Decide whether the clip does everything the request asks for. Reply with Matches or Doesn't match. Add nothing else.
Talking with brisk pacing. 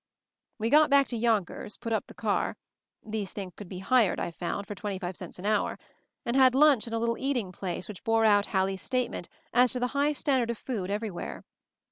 Matches